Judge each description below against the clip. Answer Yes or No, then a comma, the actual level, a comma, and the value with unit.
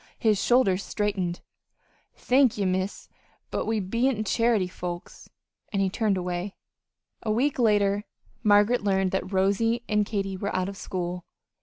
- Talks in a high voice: Yes, high, 200 Hz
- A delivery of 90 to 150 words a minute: Yes, average, 145 wpm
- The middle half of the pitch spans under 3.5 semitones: Yes, average, 2.9 semitones